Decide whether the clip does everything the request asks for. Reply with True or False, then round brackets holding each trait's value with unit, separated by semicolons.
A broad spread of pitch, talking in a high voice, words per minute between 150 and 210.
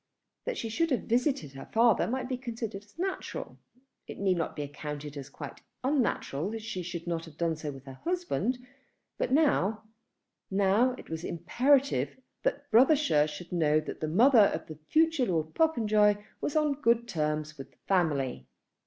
True (8.7 semitones; 200 Hz; 170 wpm)